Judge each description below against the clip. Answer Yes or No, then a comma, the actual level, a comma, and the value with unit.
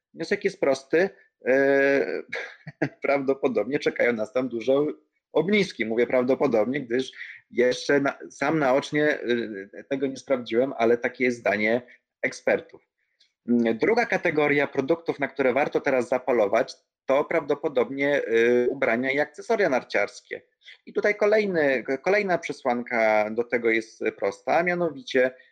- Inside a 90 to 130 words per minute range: Yes, average, 115 wpm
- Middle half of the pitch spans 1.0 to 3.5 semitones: No, average, 4.3 semitones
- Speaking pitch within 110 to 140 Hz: Yes, low, 135 Hz